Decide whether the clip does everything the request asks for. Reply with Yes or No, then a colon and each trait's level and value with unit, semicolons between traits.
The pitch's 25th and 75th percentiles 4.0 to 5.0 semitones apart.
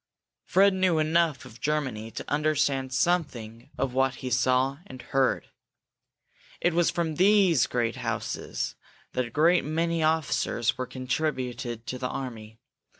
Yes: average, 4.3 semitones